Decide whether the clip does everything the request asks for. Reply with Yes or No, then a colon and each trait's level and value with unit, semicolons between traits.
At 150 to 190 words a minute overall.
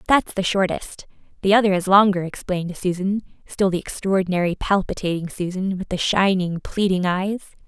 No: average, 140 wpm